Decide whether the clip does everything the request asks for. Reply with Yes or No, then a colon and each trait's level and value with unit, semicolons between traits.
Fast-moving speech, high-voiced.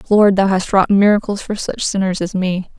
Yes: fast, 215 wpm; high, 195 Hz